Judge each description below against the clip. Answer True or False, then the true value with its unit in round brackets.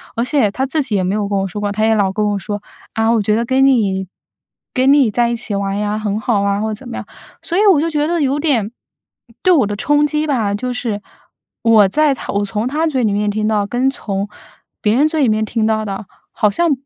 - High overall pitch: True (220 Hz)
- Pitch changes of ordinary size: True (4.5 semitones)